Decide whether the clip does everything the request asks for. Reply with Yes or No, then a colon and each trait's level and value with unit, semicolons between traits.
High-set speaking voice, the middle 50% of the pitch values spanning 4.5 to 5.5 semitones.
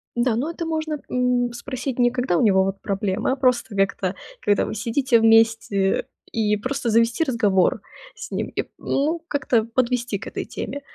No: high, 235 Hz; average, 3.7 semitones